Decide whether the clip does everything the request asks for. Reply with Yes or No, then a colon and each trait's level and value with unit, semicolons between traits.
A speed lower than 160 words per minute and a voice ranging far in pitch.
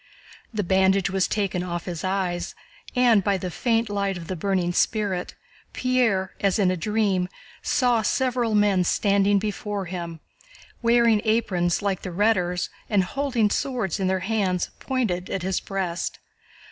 No: average, 150 wpm; average, 3.2 semitones